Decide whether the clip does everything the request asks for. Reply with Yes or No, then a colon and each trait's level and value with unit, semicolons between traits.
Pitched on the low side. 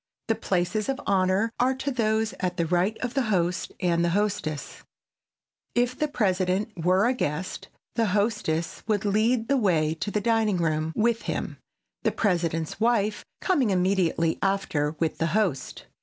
No: high, 200 Hz